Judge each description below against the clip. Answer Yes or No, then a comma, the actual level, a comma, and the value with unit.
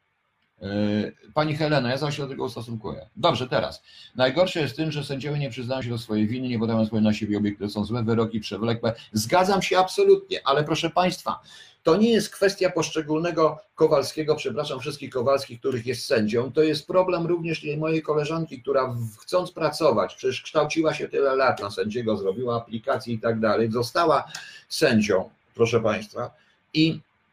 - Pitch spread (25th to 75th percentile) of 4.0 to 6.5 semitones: Yes, wide, 5.5 semitones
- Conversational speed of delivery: No, fast, 165 wpm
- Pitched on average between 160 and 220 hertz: No, medium, 140 Hz